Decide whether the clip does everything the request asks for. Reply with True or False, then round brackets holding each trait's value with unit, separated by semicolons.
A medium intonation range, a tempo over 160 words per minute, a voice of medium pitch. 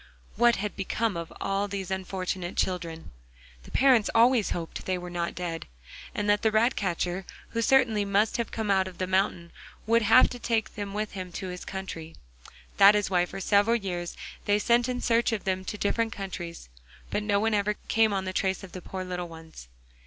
False (3.1 semitones; 200 wpm; 195 Hz)